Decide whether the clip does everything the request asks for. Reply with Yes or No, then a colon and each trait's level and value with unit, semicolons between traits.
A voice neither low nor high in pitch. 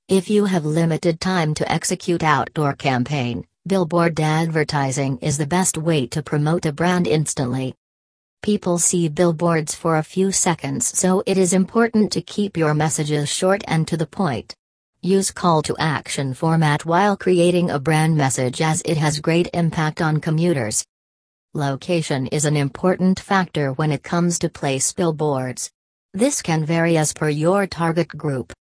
Yes: medium, 160 Hz